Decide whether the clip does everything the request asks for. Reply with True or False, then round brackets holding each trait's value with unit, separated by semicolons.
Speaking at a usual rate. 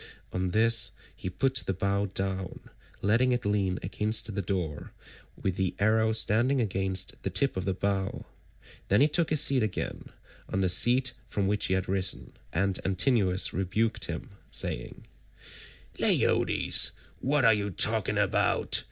True (150 wpm)